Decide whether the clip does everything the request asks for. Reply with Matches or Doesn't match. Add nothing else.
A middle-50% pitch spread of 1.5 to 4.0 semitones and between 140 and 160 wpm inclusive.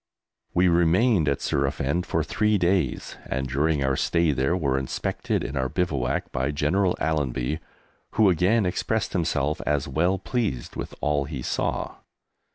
Doesn't match